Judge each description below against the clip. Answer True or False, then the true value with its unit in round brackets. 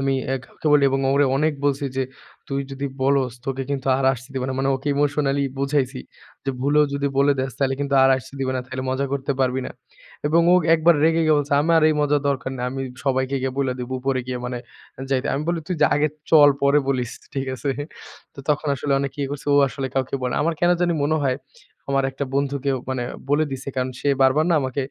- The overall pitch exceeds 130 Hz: True (140 Hz)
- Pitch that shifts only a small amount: True (1.6 semitones)